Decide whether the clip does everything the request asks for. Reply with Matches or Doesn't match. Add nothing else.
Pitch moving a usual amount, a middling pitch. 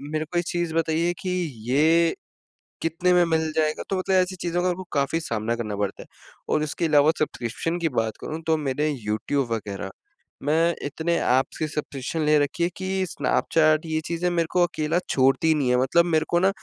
Matches